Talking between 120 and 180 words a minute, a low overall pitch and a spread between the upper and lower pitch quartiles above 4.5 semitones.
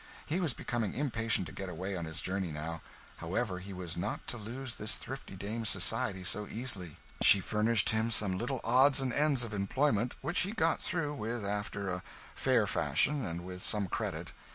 No: average, 190 wpm; low, 105 Hz; wide, 5.4 semitones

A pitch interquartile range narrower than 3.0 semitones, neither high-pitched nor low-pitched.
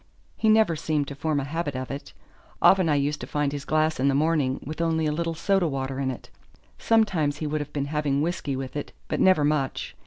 Yes: narrow, 2.6 semitones; medium, 150 Hz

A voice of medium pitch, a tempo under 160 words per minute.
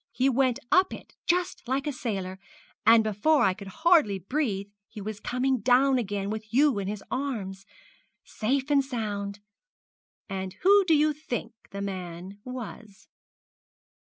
No: high, 230 Hz; average, 150 wpm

